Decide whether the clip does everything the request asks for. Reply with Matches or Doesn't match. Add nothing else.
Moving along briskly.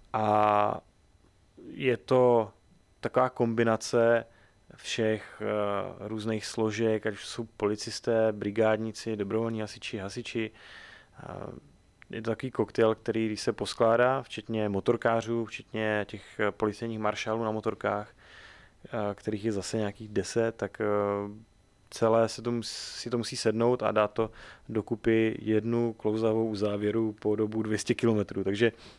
Doesn't match